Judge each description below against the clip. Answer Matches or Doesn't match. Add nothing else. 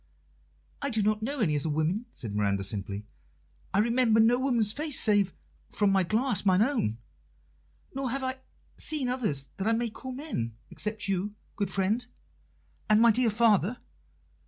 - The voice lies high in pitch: Matches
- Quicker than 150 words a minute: Matches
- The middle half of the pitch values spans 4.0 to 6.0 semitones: Matches